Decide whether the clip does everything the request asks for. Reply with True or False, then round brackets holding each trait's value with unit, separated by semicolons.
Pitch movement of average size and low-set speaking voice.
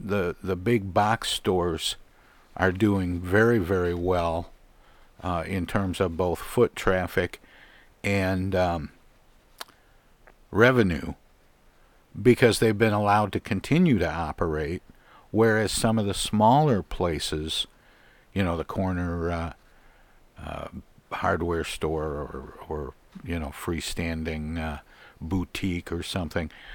True (3.5 semitones; 90 Hz)